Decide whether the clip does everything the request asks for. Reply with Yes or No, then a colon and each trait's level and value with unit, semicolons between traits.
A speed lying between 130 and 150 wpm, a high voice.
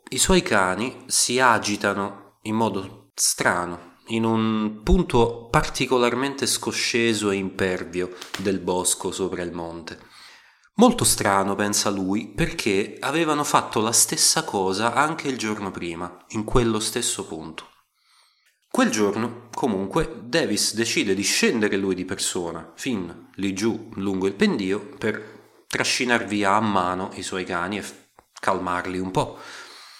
No: average, 135 wpm; low, 105 Hz